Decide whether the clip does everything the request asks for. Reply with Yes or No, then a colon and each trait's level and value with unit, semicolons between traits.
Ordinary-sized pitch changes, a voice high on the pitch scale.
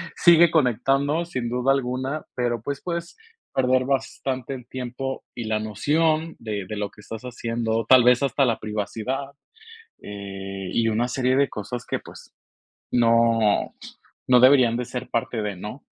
No: average, 3.3 semitones; low, 125 Hz